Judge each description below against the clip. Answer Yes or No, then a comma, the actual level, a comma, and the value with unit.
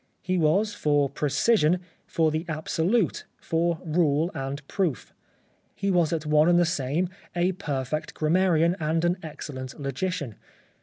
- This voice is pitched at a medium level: Yes, medium, 160 Hz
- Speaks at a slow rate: No, average, 150 wpm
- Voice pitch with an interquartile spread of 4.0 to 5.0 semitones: No, average, 3.0 semitones